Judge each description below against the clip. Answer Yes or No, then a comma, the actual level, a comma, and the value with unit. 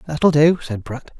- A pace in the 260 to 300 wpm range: No, average, 200 wpm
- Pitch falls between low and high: Yes, medium, 145 Hz